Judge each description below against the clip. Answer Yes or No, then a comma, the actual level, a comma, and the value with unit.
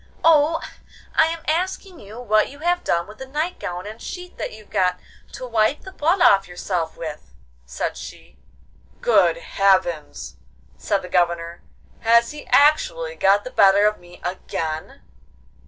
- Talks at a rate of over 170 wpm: No, average, 155 wpm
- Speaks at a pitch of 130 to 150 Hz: No, high, 210 Hz